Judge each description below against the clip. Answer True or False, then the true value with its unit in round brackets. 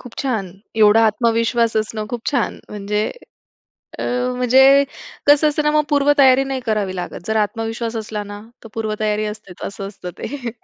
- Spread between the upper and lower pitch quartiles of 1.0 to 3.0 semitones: False (3.7 semitones)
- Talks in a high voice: True (225 Hz)